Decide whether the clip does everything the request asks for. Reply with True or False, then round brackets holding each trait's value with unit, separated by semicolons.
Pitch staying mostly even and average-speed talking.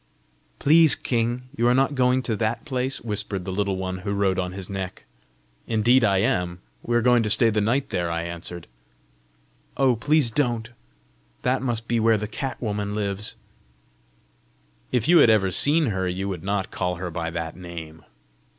False (4.7 semitones; 180 wpm)